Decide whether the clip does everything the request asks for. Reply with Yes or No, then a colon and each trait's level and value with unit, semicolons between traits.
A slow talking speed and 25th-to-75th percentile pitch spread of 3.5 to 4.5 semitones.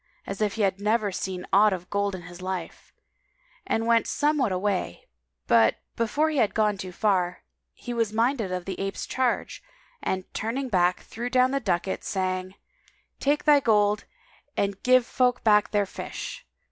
No: average, 165 wpm; average, 4.0 semitones